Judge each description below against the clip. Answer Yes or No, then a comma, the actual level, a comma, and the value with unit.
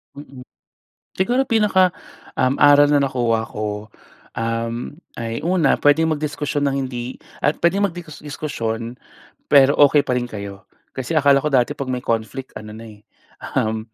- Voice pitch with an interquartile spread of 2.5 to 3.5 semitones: No, average, 4.5 semitones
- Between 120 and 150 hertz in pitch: Yes, low, 135 Hz